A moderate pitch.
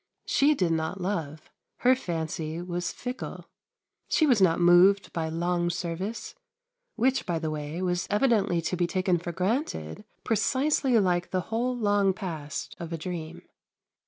Yes: medium, 180 Hz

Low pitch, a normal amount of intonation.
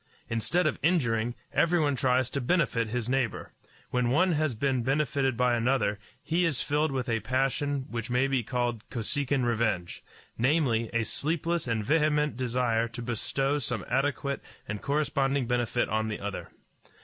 Yes: low, 130 Hz; average, 3.5 semitones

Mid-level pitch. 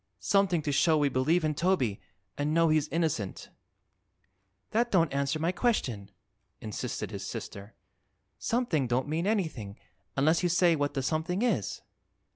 Yes: medium, 155 Hz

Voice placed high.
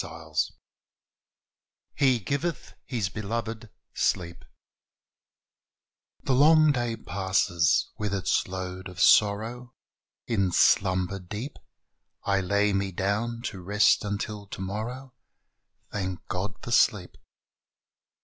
No: low, 100 Hz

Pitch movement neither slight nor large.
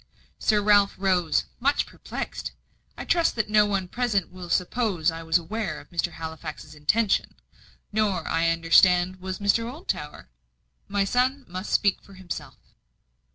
Yes: average, 4.0 semitones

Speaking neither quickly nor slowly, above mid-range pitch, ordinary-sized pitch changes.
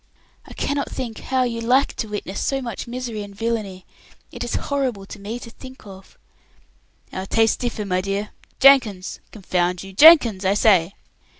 Yes: average, 160 wpm; high, 220 Hz; average, 4.3 semitones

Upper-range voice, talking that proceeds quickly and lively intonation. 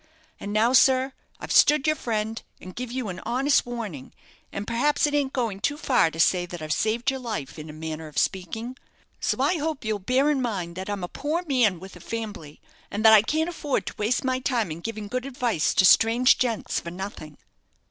Yes: high, 225 Hz; fast, 220 wpm; wide, 5.7 semitones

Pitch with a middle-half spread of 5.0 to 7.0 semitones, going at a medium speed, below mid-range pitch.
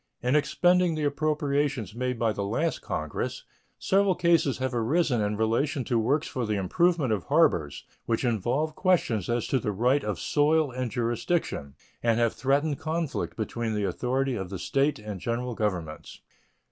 Yes: wide, 5.4 semitones; average, 165 wpm; low, 125 Hz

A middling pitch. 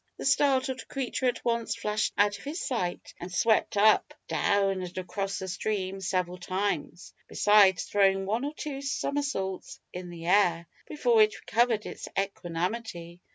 No: high, 200 Hz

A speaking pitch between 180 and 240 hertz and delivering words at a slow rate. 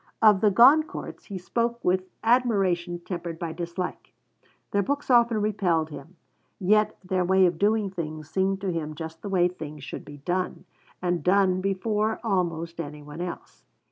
No: medium, 185 Hz; average, 165 wpm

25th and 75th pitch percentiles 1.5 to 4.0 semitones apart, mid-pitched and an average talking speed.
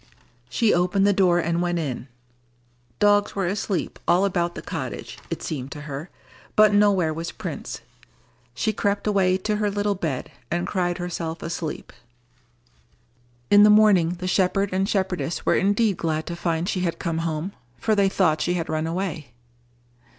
Yes: average, 3.3 semitones; medium, 180 Hz; average, 165 wpm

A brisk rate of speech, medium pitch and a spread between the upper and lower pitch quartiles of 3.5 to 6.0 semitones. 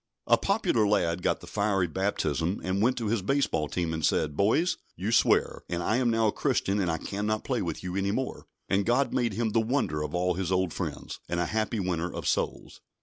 No: fast, 225 wpm; low, 100 Hz; average, 4.4 semitones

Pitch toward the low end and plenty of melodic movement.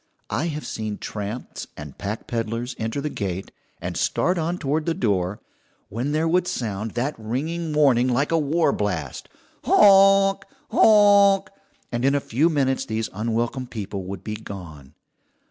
Yes: low, 125 Hz; wide, 7.0 semitones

